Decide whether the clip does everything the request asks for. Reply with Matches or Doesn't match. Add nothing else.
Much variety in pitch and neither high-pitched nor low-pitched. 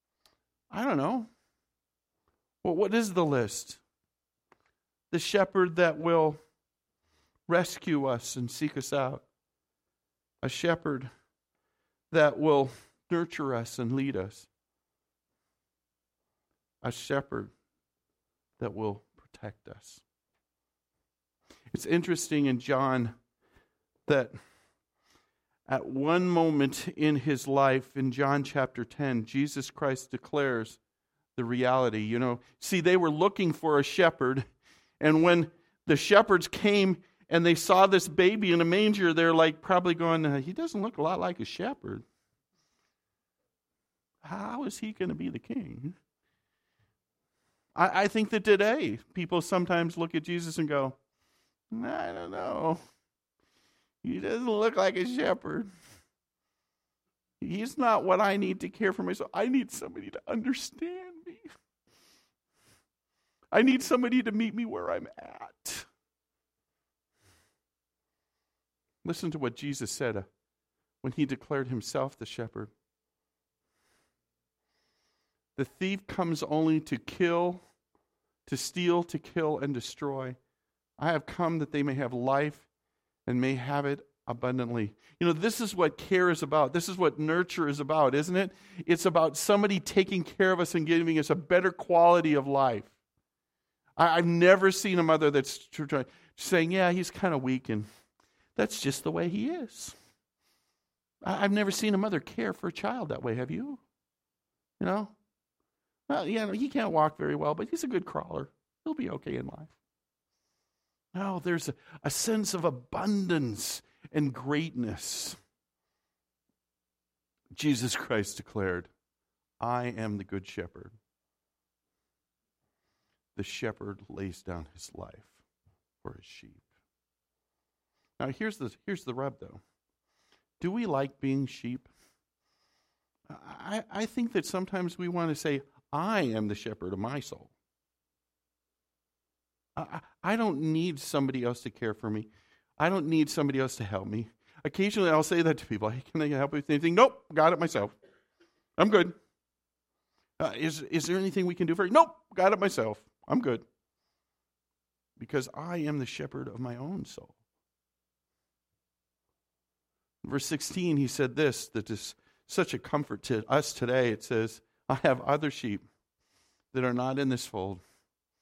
Matches